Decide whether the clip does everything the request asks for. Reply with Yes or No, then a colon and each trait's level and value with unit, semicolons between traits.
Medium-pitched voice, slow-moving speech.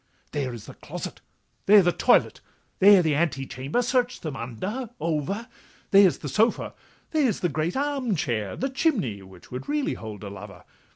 No: medium, 170 Hz; average, 160 wpm